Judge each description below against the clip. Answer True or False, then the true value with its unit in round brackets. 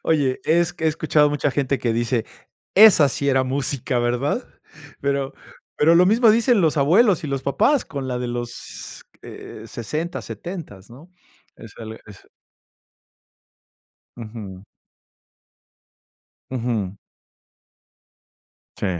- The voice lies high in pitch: False (140 Hz)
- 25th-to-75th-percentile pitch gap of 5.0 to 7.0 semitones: True (5.4 semitones)